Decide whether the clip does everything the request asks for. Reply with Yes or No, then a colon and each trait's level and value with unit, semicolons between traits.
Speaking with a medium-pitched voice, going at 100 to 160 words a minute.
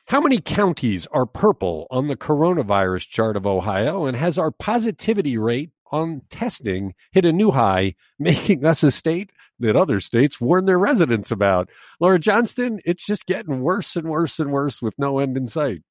No: medium, 155 Hz; average, 180 wpm